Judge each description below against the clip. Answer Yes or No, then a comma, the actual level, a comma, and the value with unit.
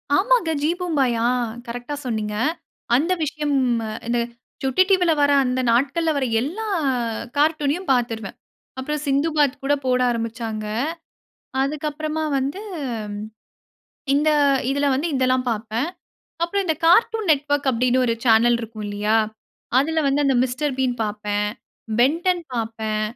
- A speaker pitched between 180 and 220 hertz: No, very high, 270 Hz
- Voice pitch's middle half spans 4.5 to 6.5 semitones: Yes, average, 4.9 semitones